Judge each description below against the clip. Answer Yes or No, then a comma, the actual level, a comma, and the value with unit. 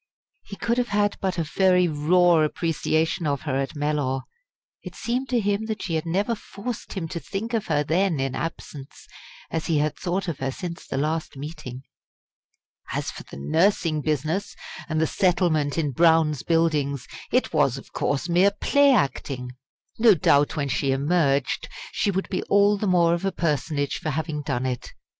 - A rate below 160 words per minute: No, average, 180 wpm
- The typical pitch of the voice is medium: Yes, medium, 165 Hz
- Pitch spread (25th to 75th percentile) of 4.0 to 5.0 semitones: Yes, average, 4.7 semitones